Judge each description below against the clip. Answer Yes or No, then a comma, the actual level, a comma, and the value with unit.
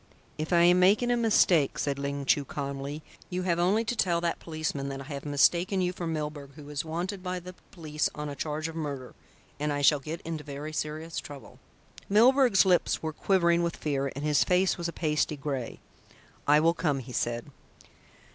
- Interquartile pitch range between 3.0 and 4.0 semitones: Yes, average, 3.7 semitones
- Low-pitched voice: No, medium, 155 Hz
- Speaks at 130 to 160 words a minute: No, average, 200 wpm